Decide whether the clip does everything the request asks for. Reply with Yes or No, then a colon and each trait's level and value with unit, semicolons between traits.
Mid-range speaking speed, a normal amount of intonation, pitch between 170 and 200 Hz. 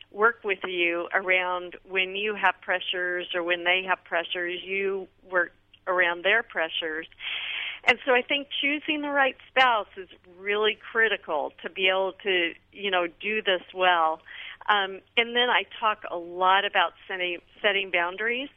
Yes: average, 160 wpm; average, 3.1 semitones; high, 190 Hz